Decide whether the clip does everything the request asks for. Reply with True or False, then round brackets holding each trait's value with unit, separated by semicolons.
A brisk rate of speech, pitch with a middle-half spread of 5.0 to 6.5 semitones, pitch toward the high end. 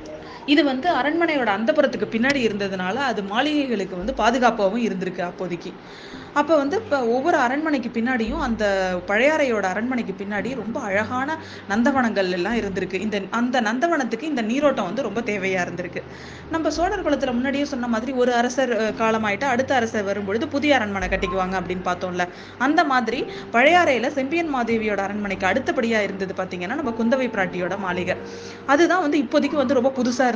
True (140 wpm; 5.6 semitones; 235 Hz)